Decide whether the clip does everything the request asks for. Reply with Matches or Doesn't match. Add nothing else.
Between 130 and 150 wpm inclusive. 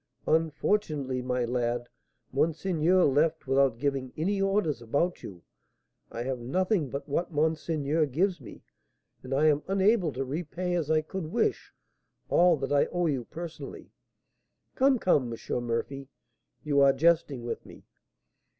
Matches